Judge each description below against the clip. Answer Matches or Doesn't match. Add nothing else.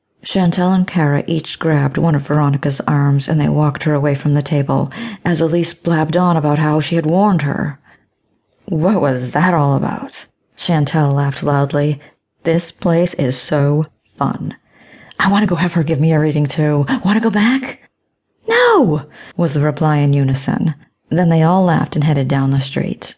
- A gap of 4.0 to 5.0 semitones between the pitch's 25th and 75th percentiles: Doesn't match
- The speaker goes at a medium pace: Matches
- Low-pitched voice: Doesn't match